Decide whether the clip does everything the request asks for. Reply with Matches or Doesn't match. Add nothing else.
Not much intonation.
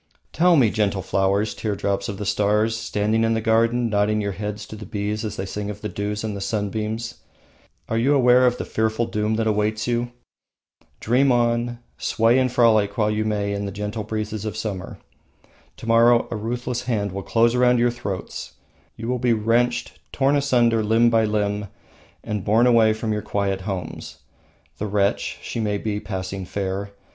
Matches